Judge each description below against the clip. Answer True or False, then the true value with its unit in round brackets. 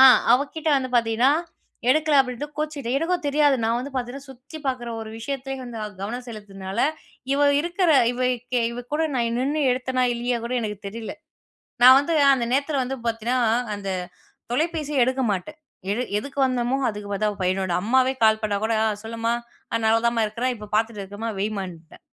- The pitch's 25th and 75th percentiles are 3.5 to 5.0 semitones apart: True (3.9 semitones)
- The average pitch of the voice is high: True (245 Hz)